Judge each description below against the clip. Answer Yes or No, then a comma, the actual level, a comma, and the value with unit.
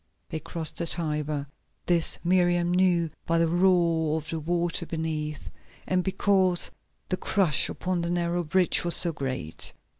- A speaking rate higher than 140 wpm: Yes, average, 150 wpm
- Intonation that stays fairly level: Yes, narrow, 2.0 semitones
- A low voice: No, medium, 170 Hz